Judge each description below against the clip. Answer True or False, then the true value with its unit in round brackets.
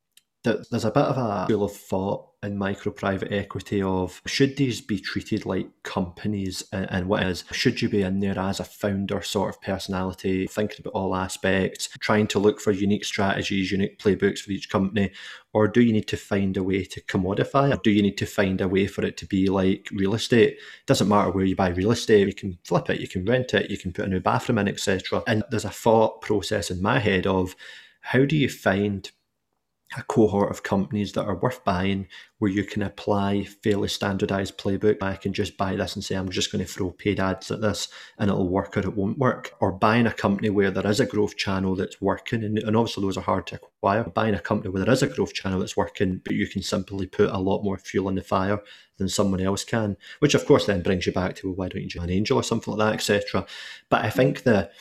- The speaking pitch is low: True (100 Hz)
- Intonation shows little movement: True (1.7 semitones)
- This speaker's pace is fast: True (240 wpm)